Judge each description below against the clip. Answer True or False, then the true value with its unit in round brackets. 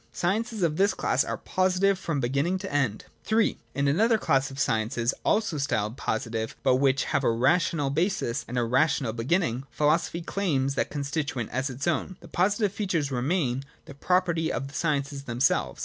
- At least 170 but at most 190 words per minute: True (175 wpm)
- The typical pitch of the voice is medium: True (145 Hz)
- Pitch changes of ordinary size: False (5.7 semitones)